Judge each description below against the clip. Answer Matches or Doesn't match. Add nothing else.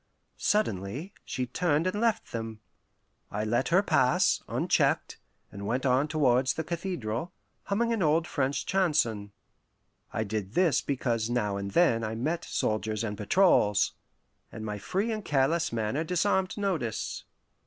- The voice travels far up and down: Matches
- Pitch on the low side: Matches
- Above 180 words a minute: Doesn't match